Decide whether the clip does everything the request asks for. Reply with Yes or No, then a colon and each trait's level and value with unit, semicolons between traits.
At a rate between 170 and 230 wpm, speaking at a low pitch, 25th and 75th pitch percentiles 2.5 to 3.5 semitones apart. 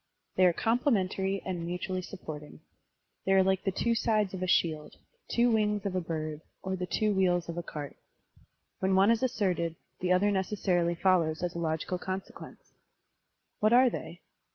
No: average, 175 wpm; medium, 185 Hz; average, 2.9 semitones